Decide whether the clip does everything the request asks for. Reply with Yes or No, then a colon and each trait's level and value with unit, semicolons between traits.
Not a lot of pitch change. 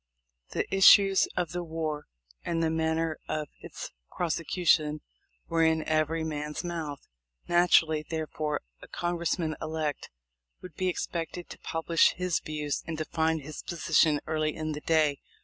Yes: narrow, 1.6 semitones